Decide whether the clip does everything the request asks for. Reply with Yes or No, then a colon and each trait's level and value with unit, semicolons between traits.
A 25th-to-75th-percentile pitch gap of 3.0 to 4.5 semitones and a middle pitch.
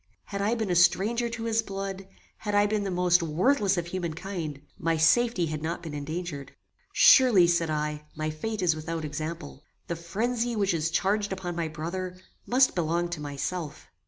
Yes: average, 4.2 semitones; medium, 175 Hz